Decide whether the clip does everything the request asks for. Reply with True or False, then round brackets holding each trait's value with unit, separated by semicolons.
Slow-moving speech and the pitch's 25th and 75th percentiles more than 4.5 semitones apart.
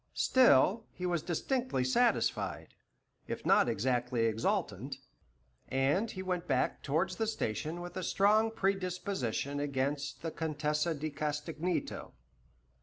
True (115 wpm; 5.5 semitones)